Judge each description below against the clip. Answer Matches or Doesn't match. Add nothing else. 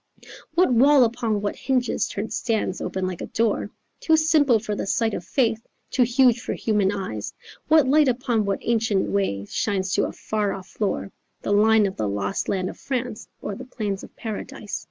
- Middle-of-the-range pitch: Doesn't match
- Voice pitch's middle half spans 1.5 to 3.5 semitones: Doesn't match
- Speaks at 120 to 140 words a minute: Doesn't match